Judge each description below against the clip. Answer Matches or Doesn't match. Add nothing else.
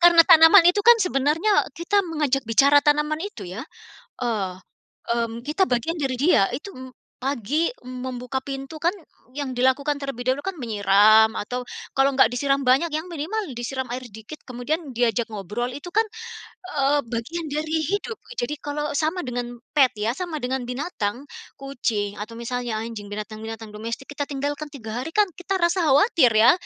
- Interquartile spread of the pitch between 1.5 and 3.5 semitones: Doesn't match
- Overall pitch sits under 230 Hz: Doesn't match